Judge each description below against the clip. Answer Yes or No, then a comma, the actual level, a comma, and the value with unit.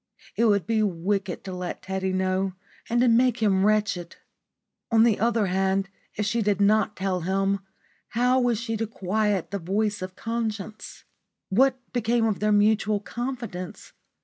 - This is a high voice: Yes, high, 210 Hz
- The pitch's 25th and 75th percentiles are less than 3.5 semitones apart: Yes, average, 2.9 semitones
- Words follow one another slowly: No, average, 160 wpm